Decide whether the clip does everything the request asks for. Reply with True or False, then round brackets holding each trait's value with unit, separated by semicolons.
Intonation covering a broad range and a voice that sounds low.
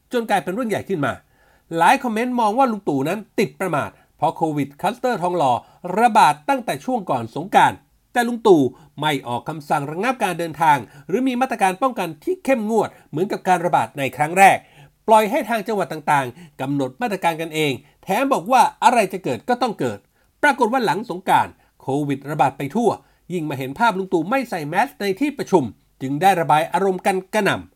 False (8.0 semitones; 185 Hz)